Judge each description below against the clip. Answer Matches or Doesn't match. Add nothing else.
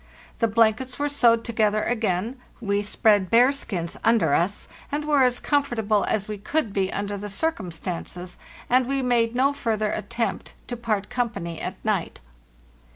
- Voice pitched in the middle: Doesn't match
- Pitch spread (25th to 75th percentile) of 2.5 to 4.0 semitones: Matches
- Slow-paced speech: Doesn't match